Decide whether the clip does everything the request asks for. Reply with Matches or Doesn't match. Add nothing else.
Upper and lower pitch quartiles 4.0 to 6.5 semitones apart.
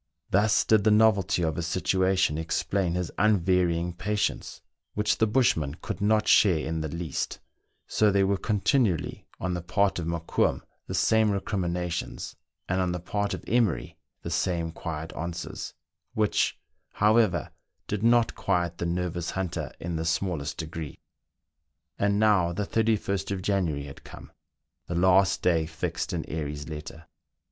Doesn't match